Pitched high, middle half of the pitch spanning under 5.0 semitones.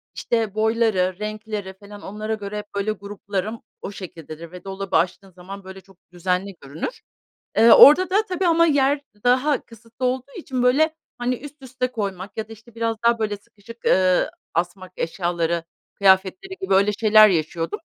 Yes: high, 210 Hz; average, 4.3 semitones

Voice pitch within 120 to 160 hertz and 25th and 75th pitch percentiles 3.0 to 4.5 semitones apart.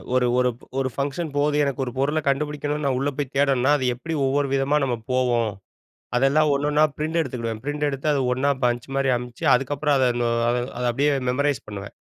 No: low, 135 Hz; narrow, 2.5 semitones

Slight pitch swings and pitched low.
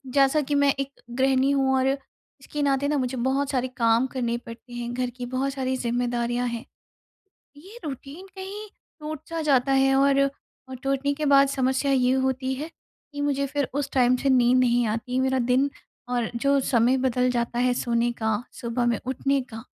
No: narrow, 2.1 semitones; very high, 265 Hz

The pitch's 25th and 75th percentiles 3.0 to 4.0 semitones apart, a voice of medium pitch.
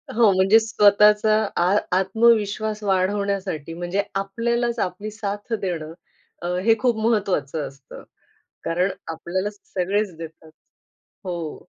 No: average, 3.4 semitones; high, 195 Hz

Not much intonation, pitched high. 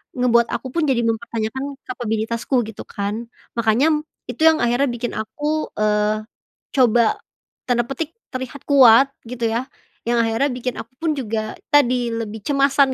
No: average, 3.3 semitones; high, 240 Hz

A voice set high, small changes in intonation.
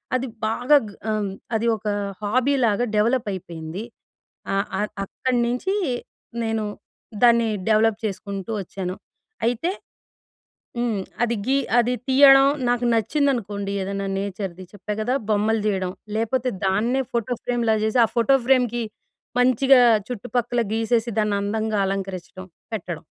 No: high, 225 Hz; average, 3.5 semitones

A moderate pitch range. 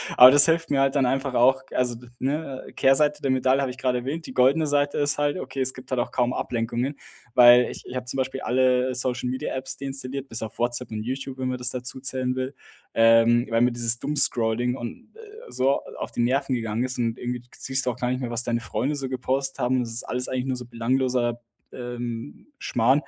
No: narrow, 1.8 semitones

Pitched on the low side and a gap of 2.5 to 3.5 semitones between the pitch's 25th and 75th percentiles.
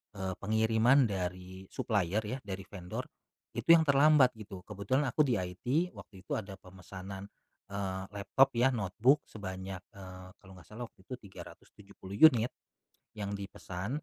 No: low, 100 Hz; average, 4.3 semitones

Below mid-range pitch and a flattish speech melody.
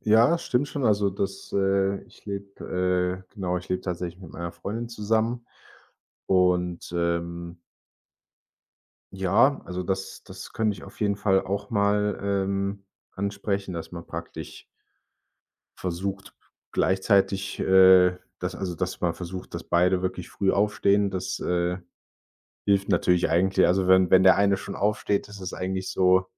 Yes: very low, 95 Hz; narrow, 1.7 semitones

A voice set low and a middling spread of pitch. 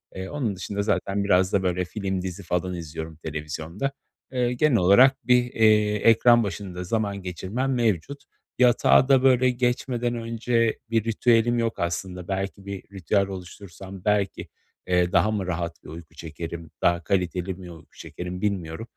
Yes: low, 100 Hz; average, 4.5 semitones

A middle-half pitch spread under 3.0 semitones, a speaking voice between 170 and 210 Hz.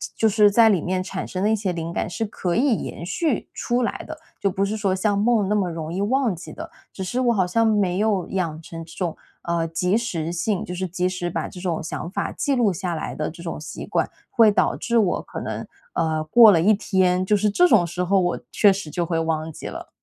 No: average, 3.8 semitones; high, 190 Hz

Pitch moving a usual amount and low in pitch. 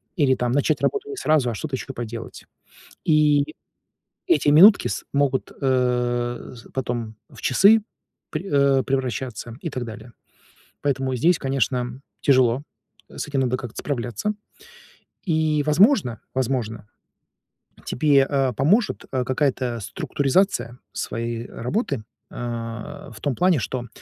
Yes: average, 3.6 semitones; low, 130 Hz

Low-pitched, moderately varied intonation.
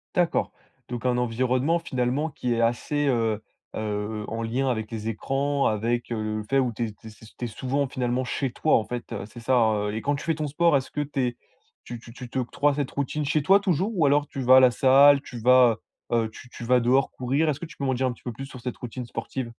Yes: low, 125 Hz; average, 3.3 semitones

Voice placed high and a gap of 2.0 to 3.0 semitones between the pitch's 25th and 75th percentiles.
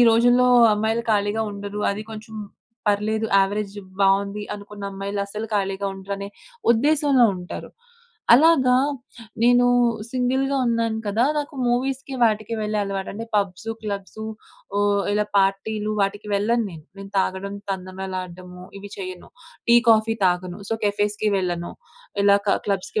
Yes: high, 205 Hz; narrow, 2.6 semitones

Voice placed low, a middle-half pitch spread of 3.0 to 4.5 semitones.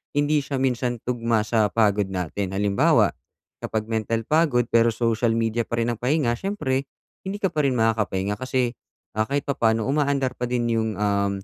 Yes: low, 115 Hz; average, 3.4 semitones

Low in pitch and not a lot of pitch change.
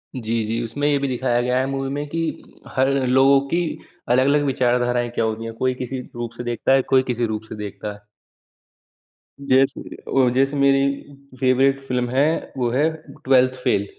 Yes: low, 130 Hz; narrow, 2.2 semitones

